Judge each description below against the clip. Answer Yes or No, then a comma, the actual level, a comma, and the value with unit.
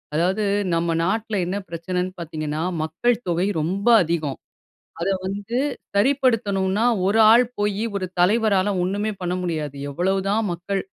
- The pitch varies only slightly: No, average, 3.4 semitones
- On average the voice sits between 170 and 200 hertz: Yes, high, 190 Hz